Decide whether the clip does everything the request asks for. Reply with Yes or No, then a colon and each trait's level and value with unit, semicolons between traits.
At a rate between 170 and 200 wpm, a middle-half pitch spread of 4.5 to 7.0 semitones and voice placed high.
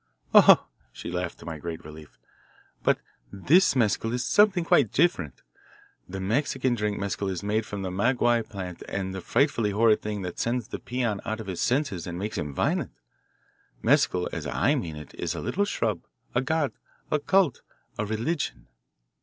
No: average, 180 wpm; wide, 5.6 semitones; low, 105 Hz